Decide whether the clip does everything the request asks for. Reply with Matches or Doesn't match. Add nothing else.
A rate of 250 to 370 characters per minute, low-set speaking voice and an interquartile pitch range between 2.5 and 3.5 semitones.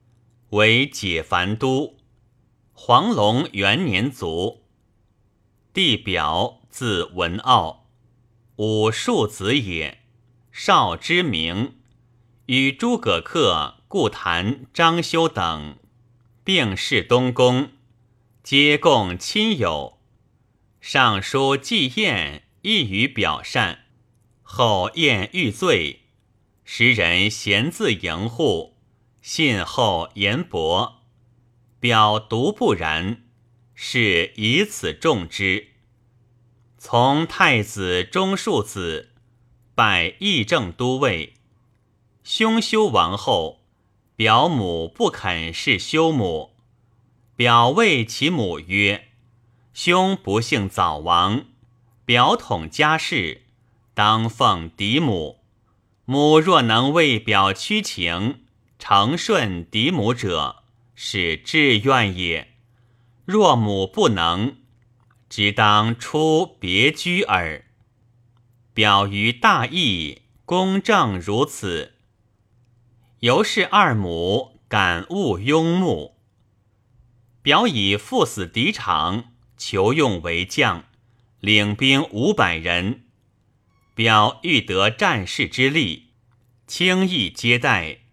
Doesn't match